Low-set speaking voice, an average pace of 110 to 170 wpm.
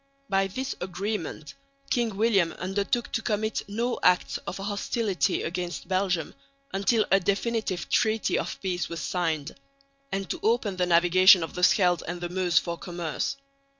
No: high, 190 Hz; average, 150 wpm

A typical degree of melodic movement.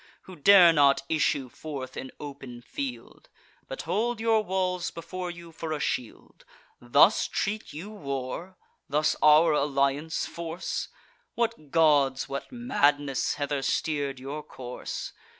Yes: average, 5.0 semitones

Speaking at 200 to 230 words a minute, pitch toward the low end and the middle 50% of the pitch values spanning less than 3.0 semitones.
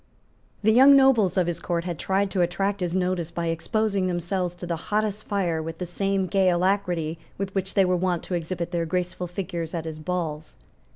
No: fast, 205 wpm; medium, 180 Hz; narrow, 2.4 semitones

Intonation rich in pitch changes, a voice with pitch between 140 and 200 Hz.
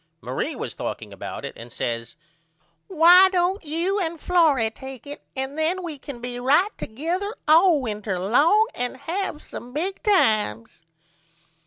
No: wide, 6.8 semitones; very high, 305 Hz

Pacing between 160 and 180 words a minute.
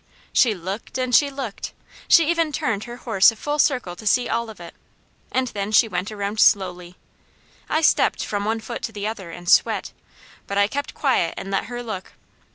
No: average, 195 wpm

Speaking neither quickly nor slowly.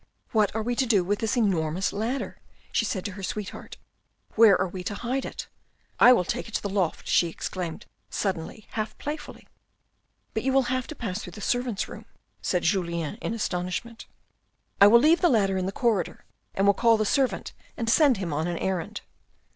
No: fast, 210 wpm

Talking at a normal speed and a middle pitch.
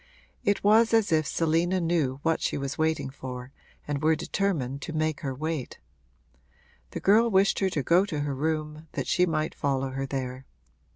Yes: average, 180 wpm; medium, 155 Hz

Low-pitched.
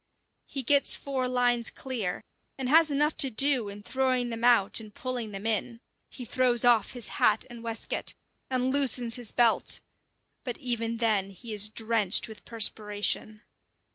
No: high, 235 Hz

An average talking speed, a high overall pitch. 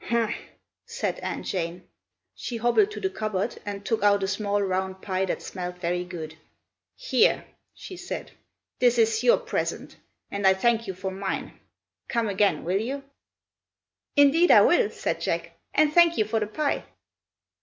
Yes: average, 165 wpm; high, 210 Hz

